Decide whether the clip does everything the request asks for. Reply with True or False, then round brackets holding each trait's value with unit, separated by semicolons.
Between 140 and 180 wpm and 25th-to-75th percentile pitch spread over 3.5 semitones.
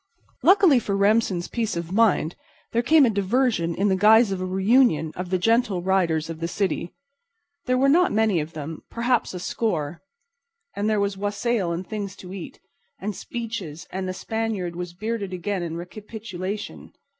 True (170 wpm; 4.3 semitones)